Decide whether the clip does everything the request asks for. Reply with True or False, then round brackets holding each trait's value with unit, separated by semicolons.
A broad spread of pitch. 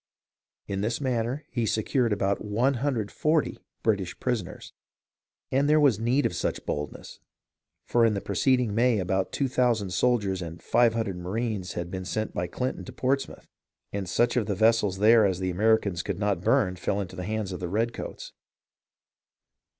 False (4.2 semitones)